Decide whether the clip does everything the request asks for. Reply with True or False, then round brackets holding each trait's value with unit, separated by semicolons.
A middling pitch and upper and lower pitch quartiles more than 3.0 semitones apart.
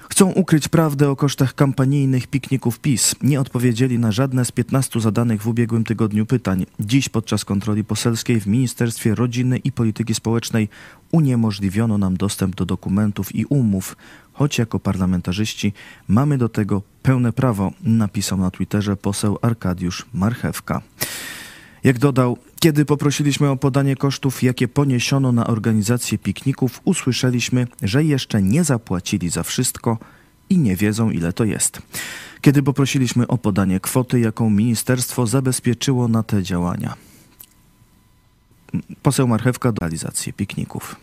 False (120 Hz; 4.0 semitones)